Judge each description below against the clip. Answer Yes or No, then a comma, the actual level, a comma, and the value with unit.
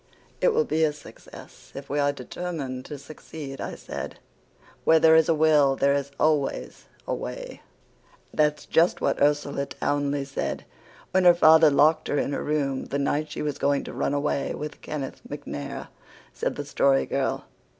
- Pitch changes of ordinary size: No, narrow, 2.1 semitones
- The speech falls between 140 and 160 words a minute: No, average, 175 wpm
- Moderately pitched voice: Yes, medium, 145 Hz